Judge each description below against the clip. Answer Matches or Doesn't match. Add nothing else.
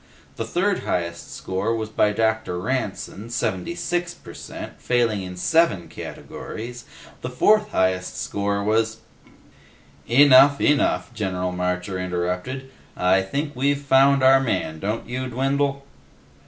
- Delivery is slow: Matches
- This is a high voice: Doesn't match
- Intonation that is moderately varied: Doesn't match